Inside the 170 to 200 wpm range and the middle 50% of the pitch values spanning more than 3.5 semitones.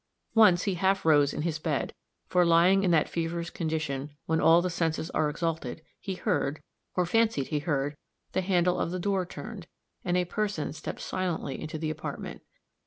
No: average, 180 wpm; average, 2.8 semitones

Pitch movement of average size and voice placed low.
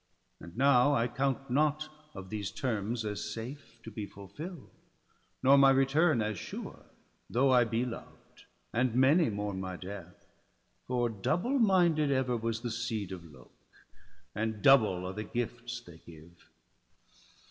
Yes: average, 5.0 semitones; low, 120 Hz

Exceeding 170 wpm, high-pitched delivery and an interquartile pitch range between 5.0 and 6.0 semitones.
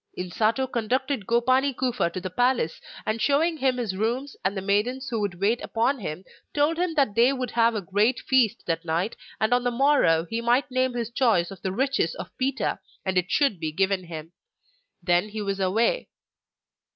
Yes: average, 195 wpm; high, 230 Hz; average, 5.3 semitones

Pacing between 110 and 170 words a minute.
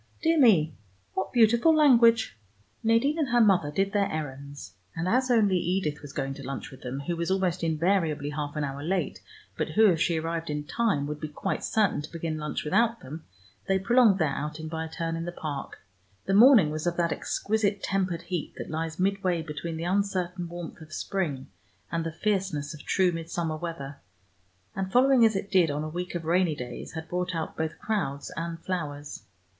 No: average, 200 wpm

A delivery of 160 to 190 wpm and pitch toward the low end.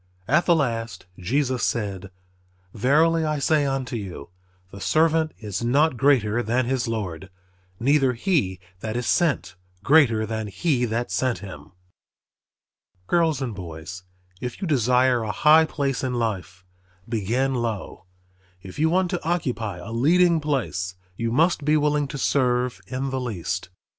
No: average, 150 wpm; low, 125 Hz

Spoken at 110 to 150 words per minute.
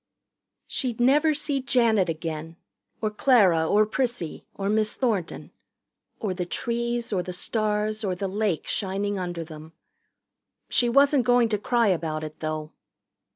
Yes: average, 145 wpm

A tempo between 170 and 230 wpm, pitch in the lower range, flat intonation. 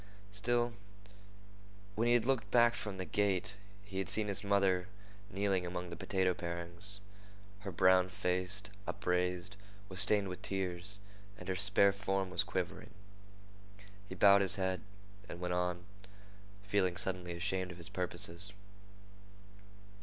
No: average, 140 wpm; very low, 95 Hz; narrow, 2.0 semitones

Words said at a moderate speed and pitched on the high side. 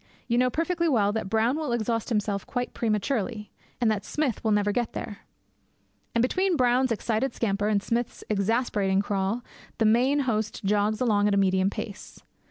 Yes: average, 175 wpm; high, 220 Hz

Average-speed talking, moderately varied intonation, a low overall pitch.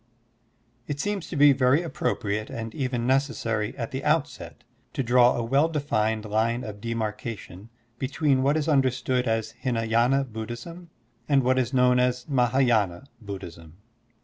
Yes: average, 145 wpm; average, 3.5 semitones; low, 125 Hz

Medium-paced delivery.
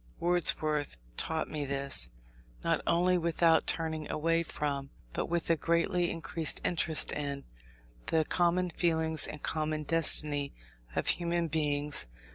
No: slow, 125 wpm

